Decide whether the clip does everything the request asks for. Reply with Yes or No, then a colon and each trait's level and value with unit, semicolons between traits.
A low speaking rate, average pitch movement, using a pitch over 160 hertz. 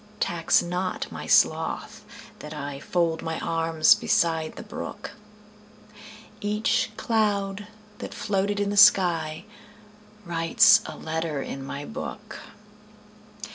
Yes: slow, 95 wpm; average, 4.4 semitones; medium, 185 Hz